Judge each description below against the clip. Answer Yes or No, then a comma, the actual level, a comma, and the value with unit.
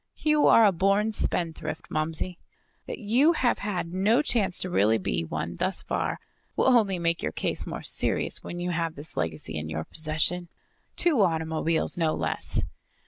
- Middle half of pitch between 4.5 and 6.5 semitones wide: Yes, average, 4.8 semitones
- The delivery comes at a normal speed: Yes, average, 170 wpm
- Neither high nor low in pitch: Yes, medium, 175 Hz